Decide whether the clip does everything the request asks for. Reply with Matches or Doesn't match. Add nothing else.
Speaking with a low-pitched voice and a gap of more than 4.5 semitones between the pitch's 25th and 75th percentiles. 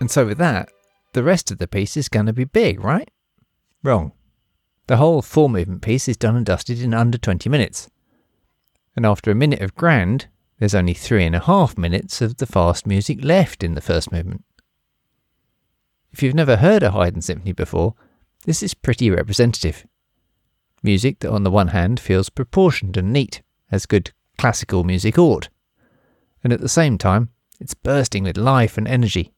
Matches